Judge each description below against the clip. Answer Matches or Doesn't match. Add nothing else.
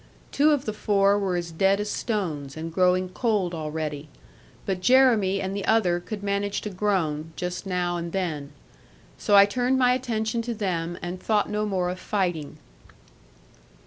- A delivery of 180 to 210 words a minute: Doesn't match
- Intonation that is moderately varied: Matches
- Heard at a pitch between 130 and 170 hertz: Doesn't match